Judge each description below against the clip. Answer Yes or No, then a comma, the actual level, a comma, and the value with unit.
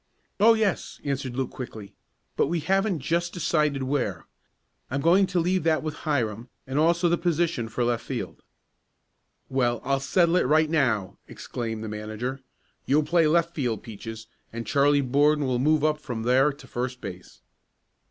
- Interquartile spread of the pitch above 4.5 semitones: Yes, average, 5.2 semitones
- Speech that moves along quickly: No, average, 165 wpm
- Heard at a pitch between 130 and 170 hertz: Yes, medium, 140 Hz